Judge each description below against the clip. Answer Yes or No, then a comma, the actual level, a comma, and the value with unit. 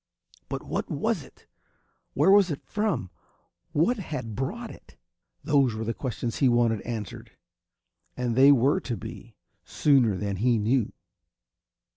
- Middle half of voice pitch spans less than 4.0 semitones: No, average, 4.7 semitones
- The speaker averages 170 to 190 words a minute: No, average, 140 wpm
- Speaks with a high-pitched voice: No, low, 125 Hz